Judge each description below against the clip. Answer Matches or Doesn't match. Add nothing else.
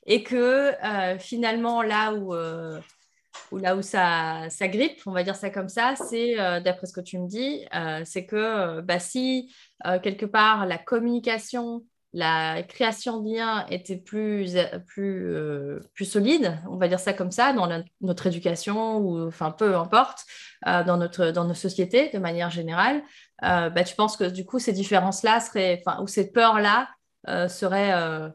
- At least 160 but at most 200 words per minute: Matches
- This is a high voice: Matches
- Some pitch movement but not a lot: Matches